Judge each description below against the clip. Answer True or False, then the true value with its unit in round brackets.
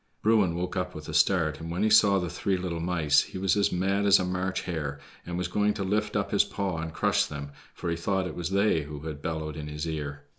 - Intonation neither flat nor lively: True (3.8 semitones)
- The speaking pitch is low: True (90 Hz)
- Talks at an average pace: False (260 wpm)